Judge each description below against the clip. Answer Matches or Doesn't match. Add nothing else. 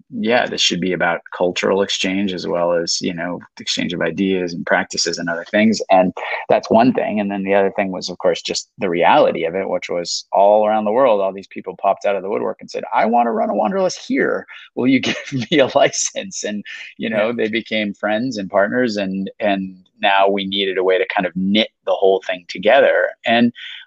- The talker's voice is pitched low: Matches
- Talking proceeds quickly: Matches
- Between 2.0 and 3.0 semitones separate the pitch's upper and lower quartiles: Matches